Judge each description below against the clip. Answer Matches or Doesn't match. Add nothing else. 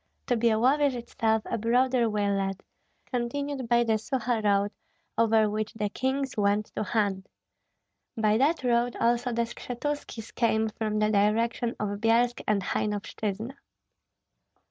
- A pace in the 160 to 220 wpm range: Doesn't match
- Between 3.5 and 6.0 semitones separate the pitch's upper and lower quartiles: Doesn't match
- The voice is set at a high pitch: Matches